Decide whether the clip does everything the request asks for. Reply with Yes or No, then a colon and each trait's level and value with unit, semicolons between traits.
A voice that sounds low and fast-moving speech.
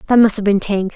No: high, 210 Hz; fast, 315 wpm